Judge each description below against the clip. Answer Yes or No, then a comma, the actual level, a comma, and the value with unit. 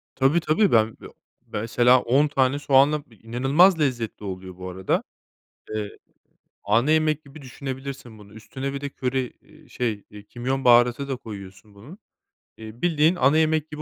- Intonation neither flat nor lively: Yes, average, 4.8 semitones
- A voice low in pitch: Yes, low, 130 Hz